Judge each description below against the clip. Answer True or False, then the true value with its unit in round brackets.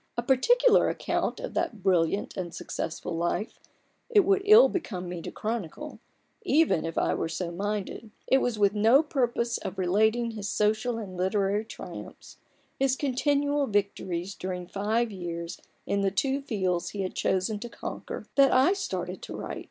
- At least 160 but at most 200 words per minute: True (165 wpm)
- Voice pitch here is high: True (215 Hz)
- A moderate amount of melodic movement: False (6.0 semitones)